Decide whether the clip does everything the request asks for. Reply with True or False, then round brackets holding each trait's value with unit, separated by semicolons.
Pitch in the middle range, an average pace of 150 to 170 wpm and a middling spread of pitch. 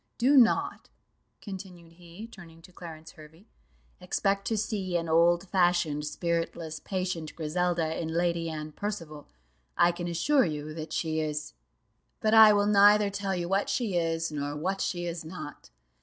True (175 Hz; 155 wpm; 3.5 semitones)